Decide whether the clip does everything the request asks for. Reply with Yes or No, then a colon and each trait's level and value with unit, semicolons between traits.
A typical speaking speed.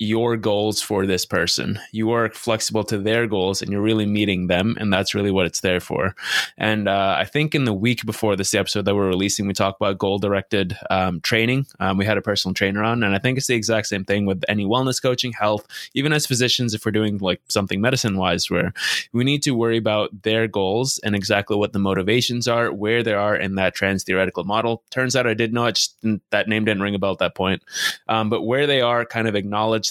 No: fast, 235 wpm